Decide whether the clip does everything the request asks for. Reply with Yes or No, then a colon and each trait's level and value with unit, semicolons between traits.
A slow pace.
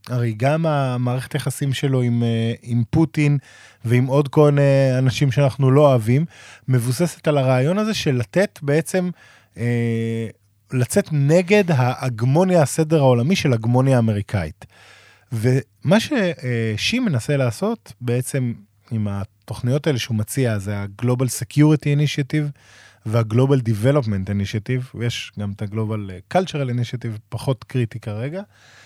No: average, 125 wpm